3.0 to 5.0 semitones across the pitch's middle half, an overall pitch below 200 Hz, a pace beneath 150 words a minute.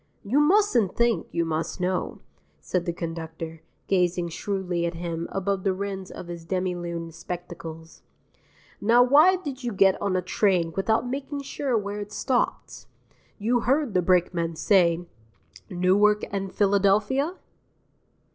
Yes: average, 4.6 semitones; high, 190 Hz; average, 140 wpm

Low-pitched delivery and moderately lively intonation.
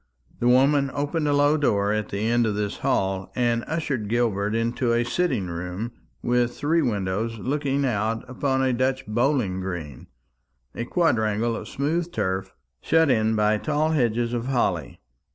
Yes: low, 120 Hz; average, 4.7 semitones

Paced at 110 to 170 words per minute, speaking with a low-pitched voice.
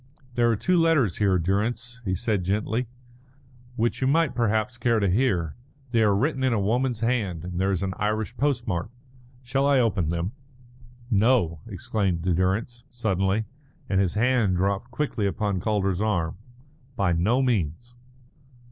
Yes: average, 155 wpm; low, 110 Hz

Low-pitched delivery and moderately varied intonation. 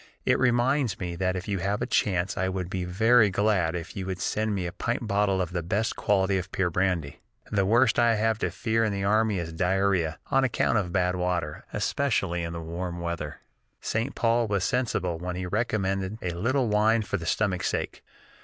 Yes: very low, 95 Hz; average, 3.6 semitones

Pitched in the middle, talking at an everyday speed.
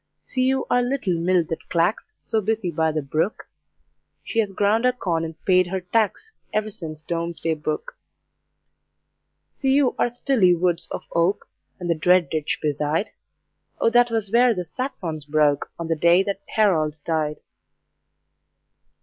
Yes: medium, 180 Hz; average, 160 wpm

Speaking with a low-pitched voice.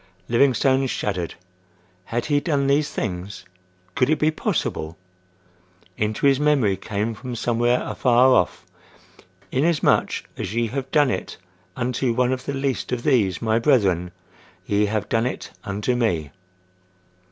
Yes: low, 120 Hz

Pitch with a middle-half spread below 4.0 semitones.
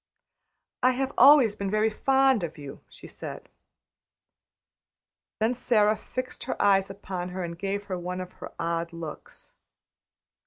No: average, 5.2 semitones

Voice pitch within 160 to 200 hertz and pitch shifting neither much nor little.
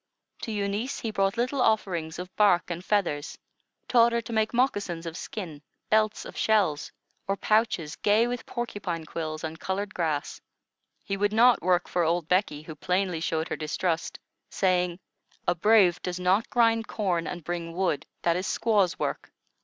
Yes: medium, 185 Hz; average, 4.2 semitones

